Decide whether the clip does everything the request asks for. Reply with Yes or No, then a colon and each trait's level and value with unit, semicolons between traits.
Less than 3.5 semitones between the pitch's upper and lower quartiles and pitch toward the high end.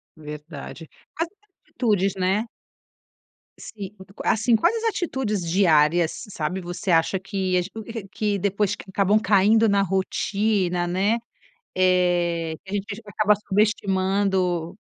Yes: average, 2.8 semitones; high, 195 Hz